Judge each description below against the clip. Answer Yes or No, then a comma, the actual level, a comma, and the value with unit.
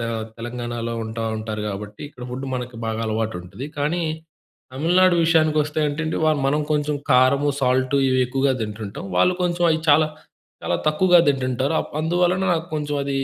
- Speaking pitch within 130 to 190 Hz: Yes, medium, 140 Hz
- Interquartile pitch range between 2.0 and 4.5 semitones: No, average, 4.9 semitones